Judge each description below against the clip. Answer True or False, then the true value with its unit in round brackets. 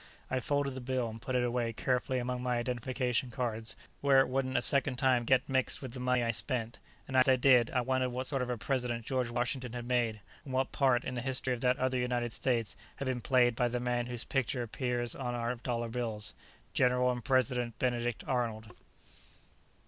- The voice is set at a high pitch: False (125 Hz)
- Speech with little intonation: True (1.4 semitones)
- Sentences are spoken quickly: True (215 wpm)